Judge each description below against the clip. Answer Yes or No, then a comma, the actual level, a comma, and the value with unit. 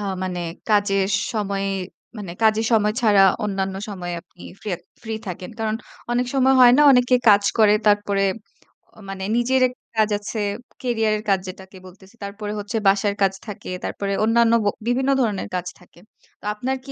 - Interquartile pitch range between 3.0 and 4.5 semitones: No, narrow, 2.6 semitones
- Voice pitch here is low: No, high, 210 Hz